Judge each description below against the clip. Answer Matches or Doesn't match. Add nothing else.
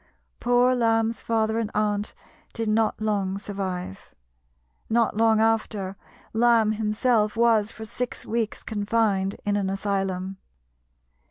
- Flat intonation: Matches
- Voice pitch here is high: Matches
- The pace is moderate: Doesn't match